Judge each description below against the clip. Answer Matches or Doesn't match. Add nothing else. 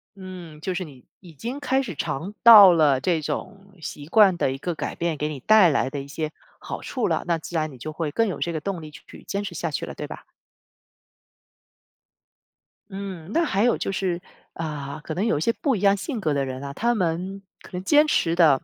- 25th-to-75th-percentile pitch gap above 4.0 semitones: Matches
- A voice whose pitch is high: Doesn't match